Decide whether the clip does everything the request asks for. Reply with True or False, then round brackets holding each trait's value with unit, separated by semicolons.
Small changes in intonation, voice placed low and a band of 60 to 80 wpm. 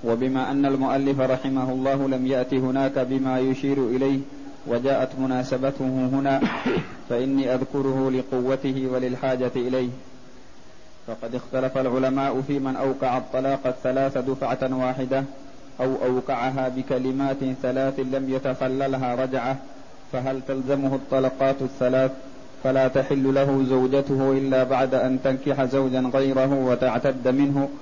False (0.8 semitones; 130 Hz; 110 wpm)